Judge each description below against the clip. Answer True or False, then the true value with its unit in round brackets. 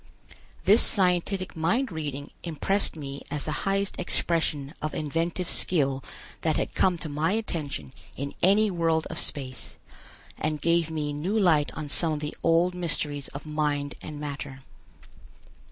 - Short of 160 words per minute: True (150 wpm)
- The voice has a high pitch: False (155 Hz)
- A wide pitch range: False (3.5 semitones)